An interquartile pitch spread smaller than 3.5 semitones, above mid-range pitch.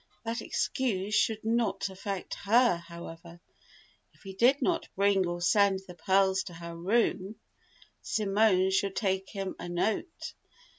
Yes: average, 2.9 semitones; high, 195 Hz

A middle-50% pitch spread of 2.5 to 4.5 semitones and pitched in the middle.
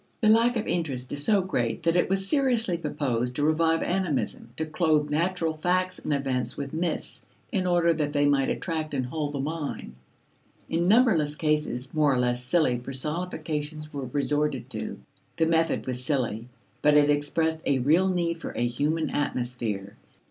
Yes: average, 3.7 semitones; medium, 150 Hz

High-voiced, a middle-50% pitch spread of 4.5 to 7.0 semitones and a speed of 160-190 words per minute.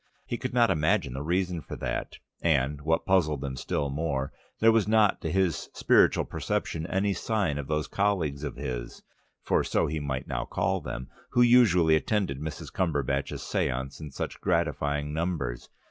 No: very low, 80 Hz; average, 5.3 semitones; average, 170 wpm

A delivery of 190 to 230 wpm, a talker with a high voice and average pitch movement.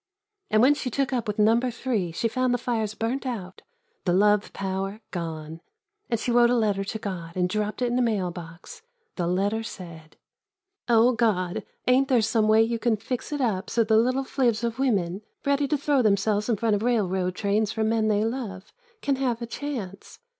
Yes: average, 200 wpm; high, 220 Hz; average, 3.9 semitones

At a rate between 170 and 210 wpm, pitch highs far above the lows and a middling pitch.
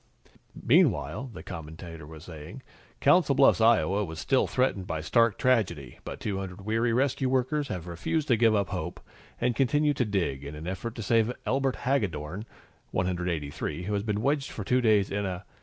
No: average, 175 wpm; wide, 6.6 semitones; low, 105 Hz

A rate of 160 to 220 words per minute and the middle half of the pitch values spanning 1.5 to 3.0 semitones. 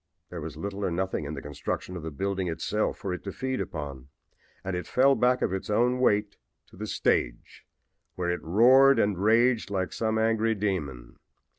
No: average, 190 wpm; average, 4.7 semitones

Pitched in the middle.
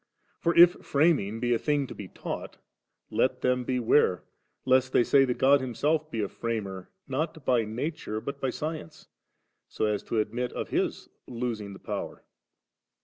No: low, 125 Hz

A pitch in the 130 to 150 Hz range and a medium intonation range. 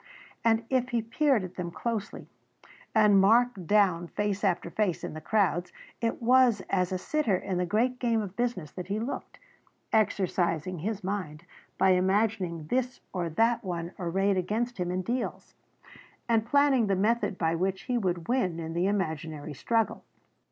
No: high, 195 Hz; average, 4.3 semitones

